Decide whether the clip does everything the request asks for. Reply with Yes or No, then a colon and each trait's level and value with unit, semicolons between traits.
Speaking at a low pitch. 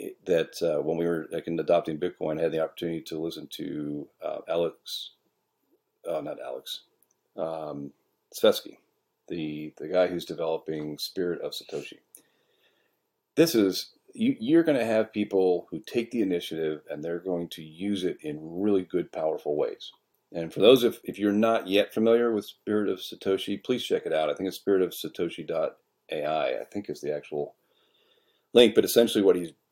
Yes: low, 100 Hz